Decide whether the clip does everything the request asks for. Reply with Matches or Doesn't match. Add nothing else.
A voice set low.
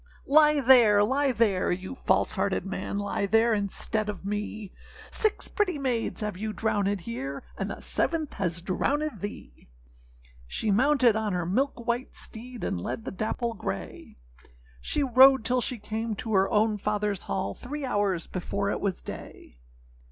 Doesn't match